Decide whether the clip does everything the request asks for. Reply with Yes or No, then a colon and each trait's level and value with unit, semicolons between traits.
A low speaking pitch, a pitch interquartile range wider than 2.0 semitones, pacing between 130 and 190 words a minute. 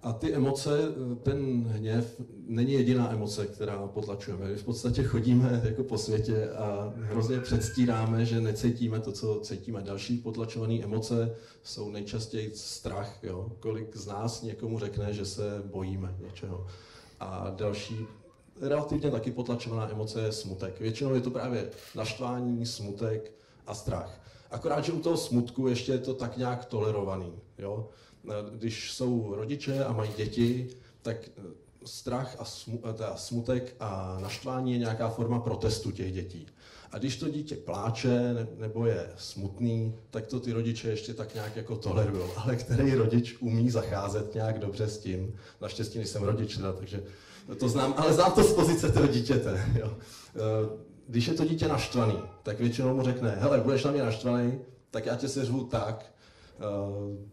Yes: low, 115 Hz; average, 2.7 semitones; average, 155 wpm